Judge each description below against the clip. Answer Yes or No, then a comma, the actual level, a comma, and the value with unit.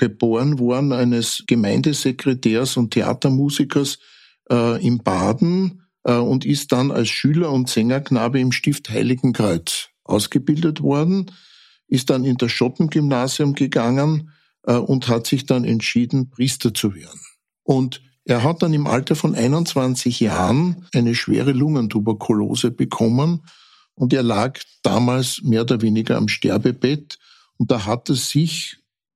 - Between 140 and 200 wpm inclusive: No, average, 130 wpm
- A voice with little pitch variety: No, average, 3.4 semitones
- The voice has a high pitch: No, low, 130 Hz